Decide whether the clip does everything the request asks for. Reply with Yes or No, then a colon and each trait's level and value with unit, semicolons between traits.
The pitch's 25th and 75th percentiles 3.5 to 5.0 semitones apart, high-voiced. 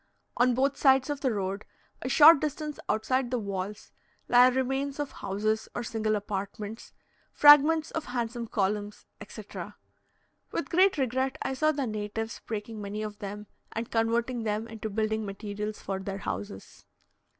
Yes: average, 4.1 semitones; high, 225 Hz